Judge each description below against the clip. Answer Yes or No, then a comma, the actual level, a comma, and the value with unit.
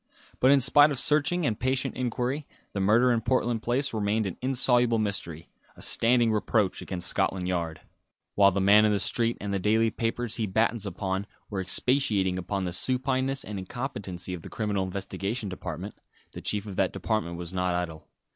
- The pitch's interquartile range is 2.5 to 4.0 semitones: No, average, 4.4 semitones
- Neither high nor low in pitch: No, low, 105 Hz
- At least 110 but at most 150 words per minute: No, average, 185 wpm